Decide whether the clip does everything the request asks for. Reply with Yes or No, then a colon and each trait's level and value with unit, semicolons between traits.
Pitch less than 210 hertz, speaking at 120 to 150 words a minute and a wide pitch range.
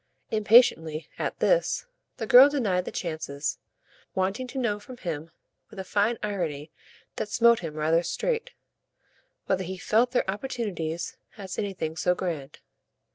Yes: high, 190 Hz; average, 140 wpm; wide, 6.2 semitones